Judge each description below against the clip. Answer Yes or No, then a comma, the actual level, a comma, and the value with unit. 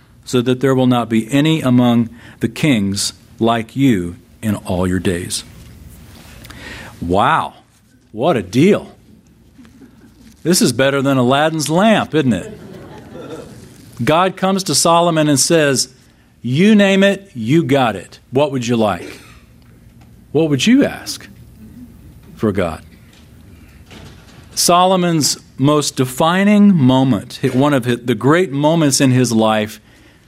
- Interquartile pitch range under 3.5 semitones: No, average, 5.2 semitones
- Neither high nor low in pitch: No, low, 130 Hz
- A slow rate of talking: Yes, slow, 125 wpm